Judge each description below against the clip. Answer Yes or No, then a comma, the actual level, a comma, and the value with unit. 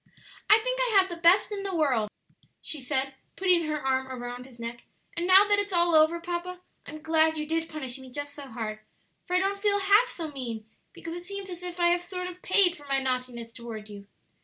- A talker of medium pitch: No, very high, 325 Hz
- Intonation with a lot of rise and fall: Yes, wide, 5.7 semitones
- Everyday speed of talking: No, fast, 230 wpm